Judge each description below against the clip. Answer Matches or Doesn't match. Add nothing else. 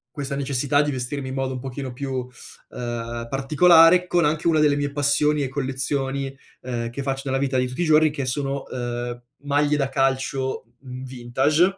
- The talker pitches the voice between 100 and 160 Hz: Matches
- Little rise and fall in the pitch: Matches